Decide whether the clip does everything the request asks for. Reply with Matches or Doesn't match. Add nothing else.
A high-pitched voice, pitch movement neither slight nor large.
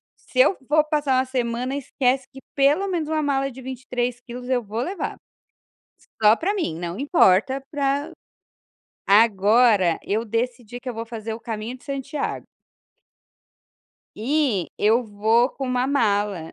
Matches